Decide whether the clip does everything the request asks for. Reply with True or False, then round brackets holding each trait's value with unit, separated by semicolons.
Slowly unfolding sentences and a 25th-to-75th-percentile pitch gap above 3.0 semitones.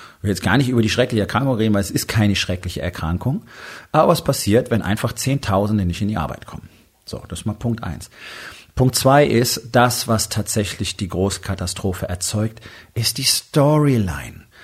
False (185 wpm; 4.2 semitones)